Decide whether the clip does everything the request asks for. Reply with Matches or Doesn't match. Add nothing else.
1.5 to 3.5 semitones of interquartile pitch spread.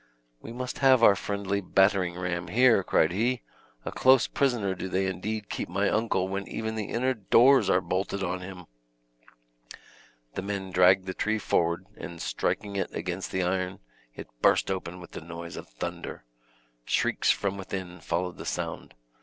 Matches